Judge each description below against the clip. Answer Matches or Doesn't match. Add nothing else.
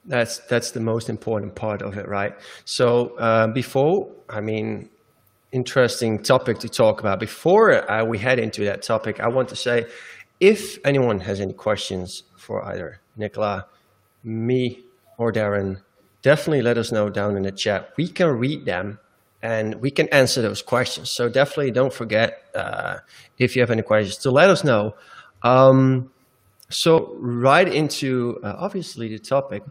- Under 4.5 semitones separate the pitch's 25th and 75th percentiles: Matches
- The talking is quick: Doesn't match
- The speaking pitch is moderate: Doesn't match